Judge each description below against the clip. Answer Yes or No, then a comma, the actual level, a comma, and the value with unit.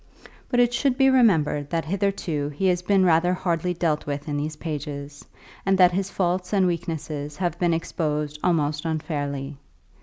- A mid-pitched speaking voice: Yes, medium, 165 Hz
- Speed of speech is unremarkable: Yes, average, 170 wpm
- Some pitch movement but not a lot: Yes, average, 3.6 semitones